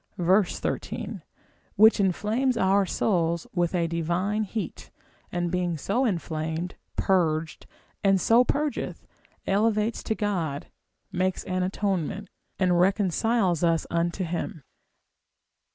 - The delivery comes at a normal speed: No, slow, 105 wpm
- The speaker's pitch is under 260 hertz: Yes, medium, 185 Hz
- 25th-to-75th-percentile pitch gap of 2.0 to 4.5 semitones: Yes, average, 3.5 semitones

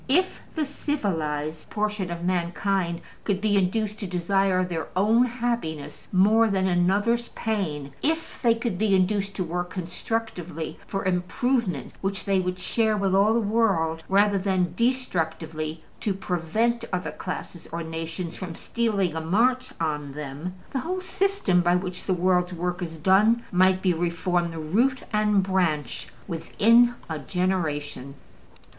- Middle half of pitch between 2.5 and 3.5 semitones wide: No, average, 4.2 semitones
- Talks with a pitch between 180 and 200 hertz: Yes, medium, 185 Hz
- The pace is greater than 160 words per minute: No, average, 145 wpm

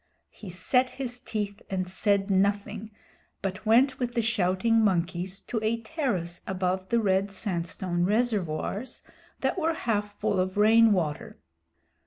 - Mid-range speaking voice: No, high, 205 Hz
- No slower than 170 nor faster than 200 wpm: No, average, 140 wpm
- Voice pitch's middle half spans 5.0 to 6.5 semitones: No, average, 3.6 semitones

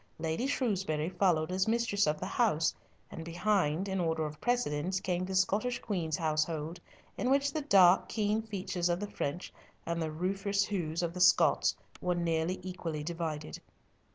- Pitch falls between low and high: Yes, medium, 180 Hz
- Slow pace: No, average, 165 wpm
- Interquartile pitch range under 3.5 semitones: No, average, 3.8 semitones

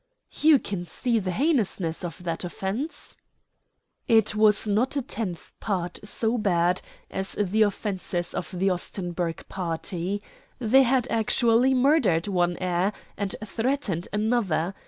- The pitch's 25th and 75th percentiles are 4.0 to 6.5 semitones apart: Yes, average, 4.5 semitones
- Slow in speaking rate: Yes, slow, 130 wpm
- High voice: Yes, high, 200 Hz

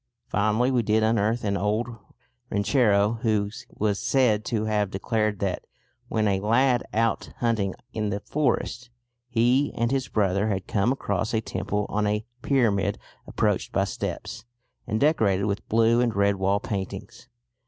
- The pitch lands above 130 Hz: No, low, 110 Hz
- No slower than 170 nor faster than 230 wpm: No, average, 155 wpm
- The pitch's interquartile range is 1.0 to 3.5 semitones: Yes, narrow, 2.5 semitones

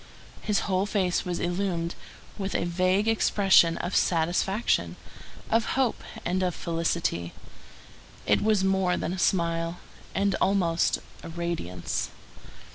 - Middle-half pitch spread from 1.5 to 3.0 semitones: Yes, narrow, 2.6 semitones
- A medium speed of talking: No, slow, 120 wpm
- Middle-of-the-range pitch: Yes, medium, 180 Hz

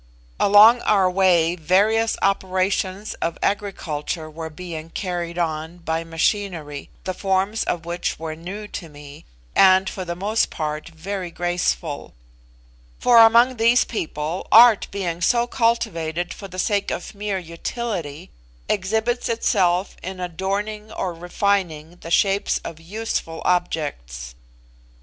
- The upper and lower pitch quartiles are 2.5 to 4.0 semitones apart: Yes, average, 3.7 semitones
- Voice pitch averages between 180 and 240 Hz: Yes, medium, 185 Hz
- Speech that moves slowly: Yes, slow, 125 wpm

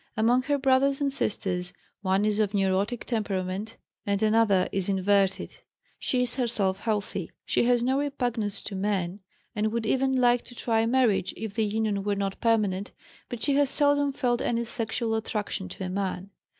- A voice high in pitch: Yes, high, 220 Hz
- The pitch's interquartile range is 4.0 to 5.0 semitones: No, average, 3.6 semitones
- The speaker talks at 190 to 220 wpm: No, average, 175 wpm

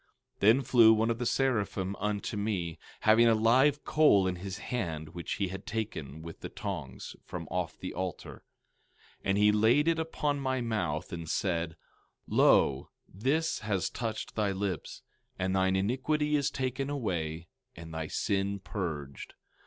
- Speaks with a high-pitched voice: No, low, 100 Hz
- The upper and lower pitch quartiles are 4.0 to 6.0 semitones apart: Yes, wide, 5.6 semitones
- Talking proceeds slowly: No, average, 160 wpm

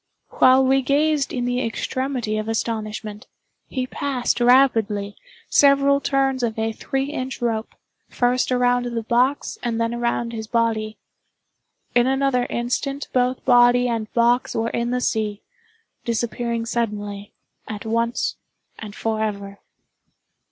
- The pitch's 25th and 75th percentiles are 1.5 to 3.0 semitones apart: Yes, narrow, 2.6 semitones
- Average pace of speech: No, slow, 125 wpm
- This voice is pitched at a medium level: No, high, 240 Hz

